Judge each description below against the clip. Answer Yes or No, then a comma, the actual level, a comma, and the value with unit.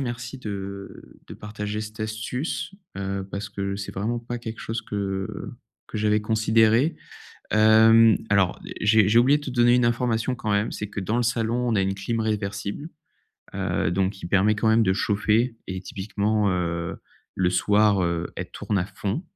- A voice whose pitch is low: Yes, low, 105 Hz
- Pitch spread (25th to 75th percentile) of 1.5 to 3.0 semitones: Yes, narrow, 2.6 semitones